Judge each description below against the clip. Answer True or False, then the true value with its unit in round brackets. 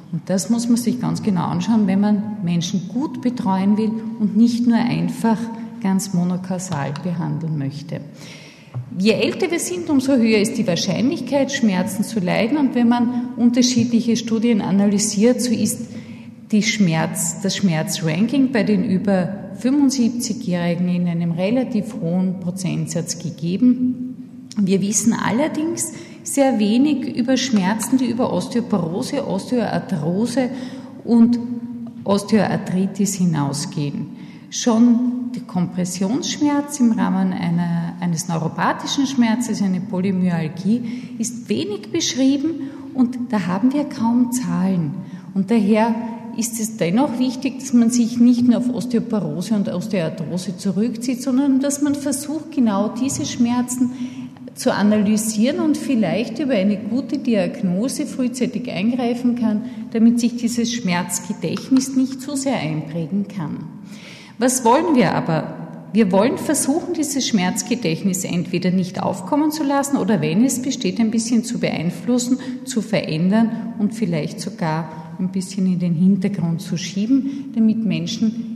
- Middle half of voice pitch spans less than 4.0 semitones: False (4.5 semitones)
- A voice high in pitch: True (225 Hz)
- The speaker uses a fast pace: False (130 wpm)